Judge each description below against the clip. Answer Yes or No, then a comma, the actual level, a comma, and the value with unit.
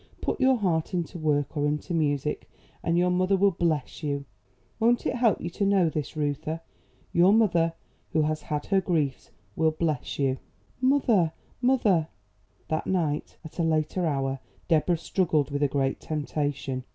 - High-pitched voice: No, medium, 160 Hz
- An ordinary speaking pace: Yes, average, 165 wpm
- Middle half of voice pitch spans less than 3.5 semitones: No, average, 3.8 semitones